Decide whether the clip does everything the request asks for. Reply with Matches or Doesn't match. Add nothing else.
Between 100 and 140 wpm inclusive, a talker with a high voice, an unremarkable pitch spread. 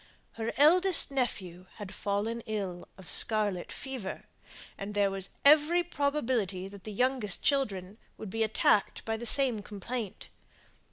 Matches